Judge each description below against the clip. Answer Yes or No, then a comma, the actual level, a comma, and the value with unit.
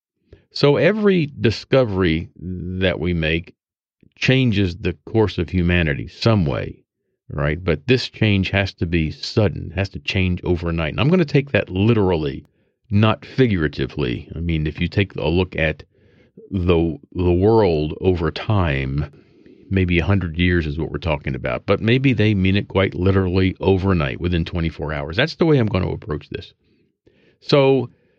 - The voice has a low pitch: Yes, very low, 90 Hz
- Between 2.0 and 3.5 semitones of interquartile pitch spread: No, average, 3.9 semitones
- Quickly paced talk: No, average, 160 wpm